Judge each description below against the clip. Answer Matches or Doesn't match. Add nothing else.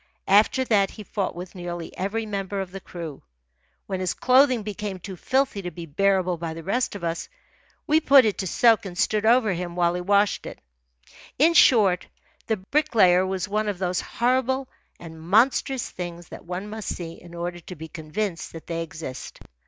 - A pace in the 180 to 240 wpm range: Matches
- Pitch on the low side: Doesn't match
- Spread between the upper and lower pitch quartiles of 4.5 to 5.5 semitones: Doesn't match